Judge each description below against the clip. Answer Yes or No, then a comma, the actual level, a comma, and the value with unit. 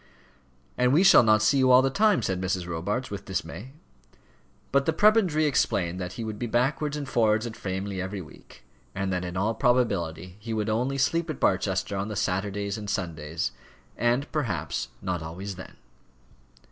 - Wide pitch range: Yes, wide, 5.7 semitones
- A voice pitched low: Yes, low, 105 Hz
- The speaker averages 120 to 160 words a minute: No, average, 180 wpm